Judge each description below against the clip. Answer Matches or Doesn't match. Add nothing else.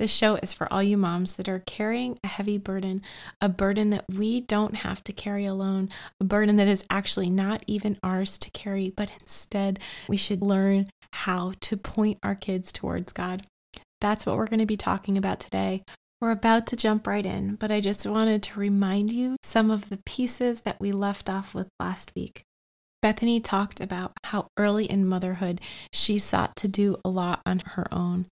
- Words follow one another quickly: Doesn't match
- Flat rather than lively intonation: Matches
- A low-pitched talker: Doesn't match